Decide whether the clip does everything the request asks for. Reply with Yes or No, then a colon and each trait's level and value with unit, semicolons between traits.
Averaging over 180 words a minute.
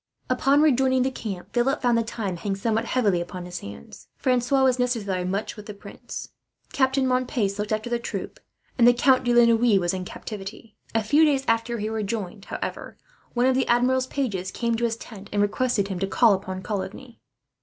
Yes: average, 200 wpm